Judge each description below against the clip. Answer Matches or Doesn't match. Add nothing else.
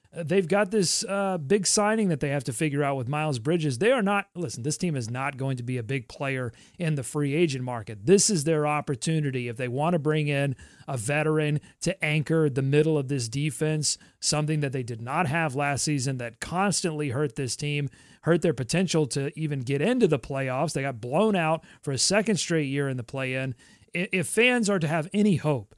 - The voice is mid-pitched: Matches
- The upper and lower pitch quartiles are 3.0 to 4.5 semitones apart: Matches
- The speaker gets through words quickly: Matches